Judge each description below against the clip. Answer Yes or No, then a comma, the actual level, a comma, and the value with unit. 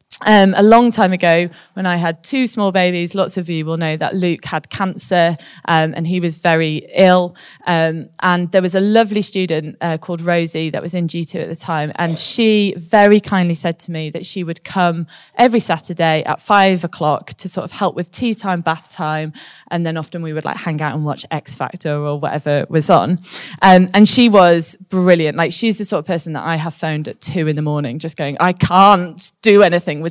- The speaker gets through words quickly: Yes, fast, 220 wpm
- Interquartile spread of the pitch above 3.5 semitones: No, average, 2.8 semitones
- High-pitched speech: No, medium, 175 Hz